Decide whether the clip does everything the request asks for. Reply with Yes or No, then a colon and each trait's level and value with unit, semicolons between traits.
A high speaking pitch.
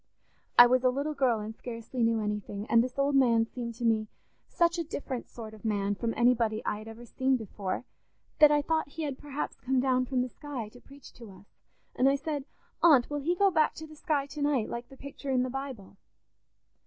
Yes: very high, 255 Hz